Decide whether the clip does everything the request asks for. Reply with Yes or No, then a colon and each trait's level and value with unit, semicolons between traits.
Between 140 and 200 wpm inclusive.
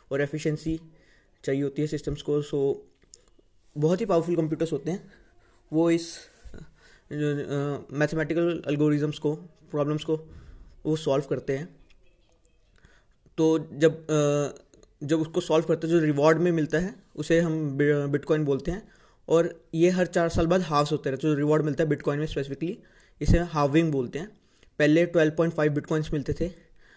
Yes: average, 150 wpm